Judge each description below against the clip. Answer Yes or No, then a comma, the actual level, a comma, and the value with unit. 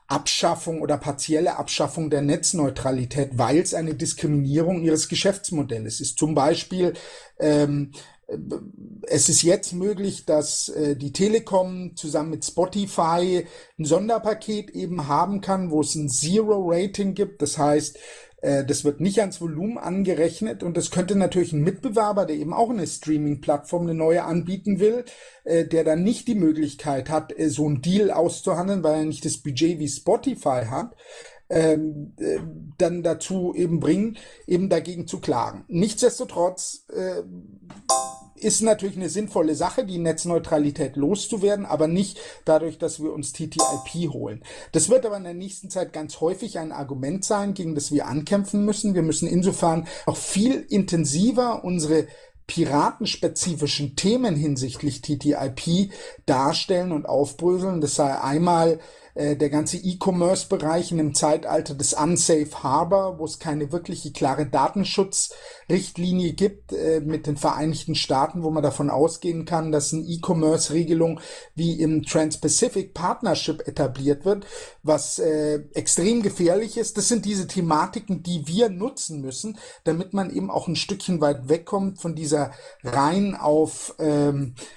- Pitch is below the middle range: No, medium, 165 Hz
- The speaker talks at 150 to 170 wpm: No, average, 140 wpm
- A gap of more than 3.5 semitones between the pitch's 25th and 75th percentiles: Yes, average, 4.2 semitones